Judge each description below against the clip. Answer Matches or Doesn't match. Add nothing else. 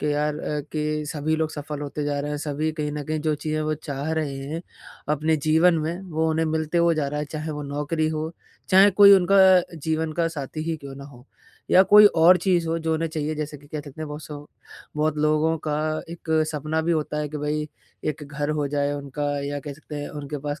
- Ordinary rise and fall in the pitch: Doesn't match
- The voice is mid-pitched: Matches